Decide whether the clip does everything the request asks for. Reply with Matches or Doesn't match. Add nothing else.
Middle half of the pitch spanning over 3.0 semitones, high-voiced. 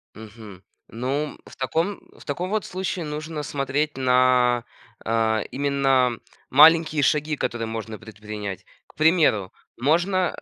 Doesn't match